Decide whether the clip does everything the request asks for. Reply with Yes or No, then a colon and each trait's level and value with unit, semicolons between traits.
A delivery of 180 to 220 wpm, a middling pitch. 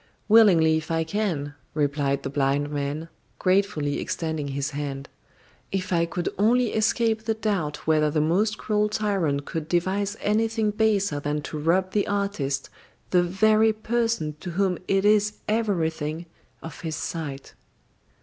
No: average, 145 wpm; medium, 175 Hz